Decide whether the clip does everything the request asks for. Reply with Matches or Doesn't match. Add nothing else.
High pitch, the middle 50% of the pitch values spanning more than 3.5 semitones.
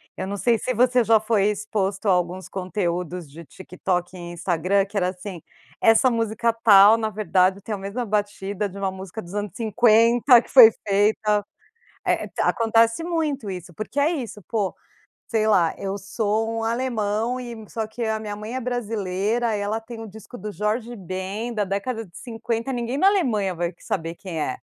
Doesn't match